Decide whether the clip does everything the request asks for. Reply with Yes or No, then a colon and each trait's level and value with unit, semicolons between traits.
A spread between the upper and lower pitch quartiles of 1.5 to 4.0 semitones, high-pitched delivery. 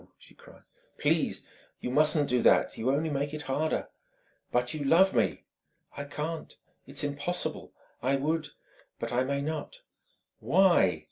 No: narrow, 2.6 semitones; medium, 145 Hz